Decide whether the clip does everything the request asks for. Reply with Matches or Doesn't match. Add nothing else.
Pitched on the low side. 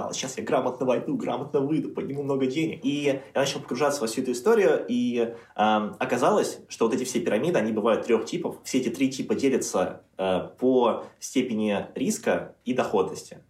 Matches